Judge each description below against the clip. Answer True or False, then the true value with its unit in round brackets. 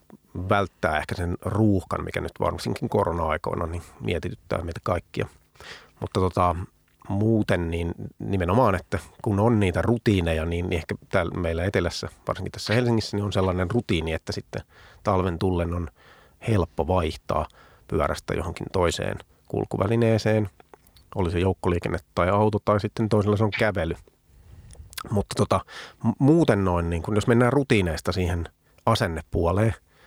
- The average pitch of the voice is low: True (95 Hz)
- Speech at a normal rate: True (135 wpm)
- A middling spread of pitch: True (3.7 semitones)